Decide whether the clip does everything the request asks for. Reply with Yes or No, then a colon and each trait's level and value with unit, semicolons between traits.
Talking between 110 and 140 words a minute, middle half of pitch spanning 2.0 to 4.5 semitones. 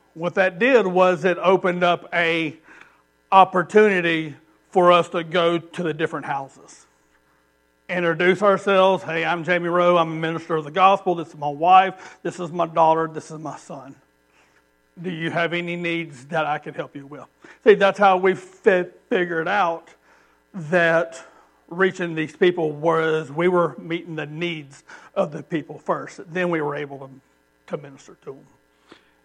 No: average, 170 wpm; average, 3.0 semitones